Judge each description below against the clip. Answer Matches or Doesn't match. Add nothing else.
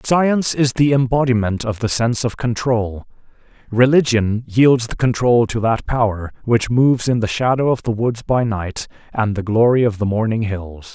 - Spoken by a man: Matches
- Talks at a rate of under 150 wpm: Doesn't match